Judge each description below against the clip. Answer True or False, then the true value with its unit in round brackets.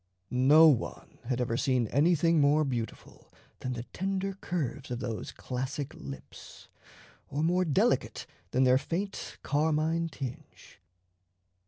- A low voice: False (145 Hz)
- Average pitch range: True (4.5 semitones)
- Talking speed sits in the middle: False (125 wpm)